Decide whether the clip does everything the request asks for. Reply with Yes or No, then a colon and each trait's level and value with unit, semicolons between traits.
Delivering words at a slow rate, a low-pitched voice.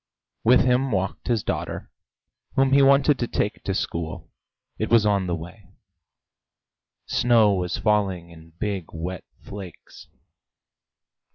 Yes: slow, 125 wpm; low, 105 Hz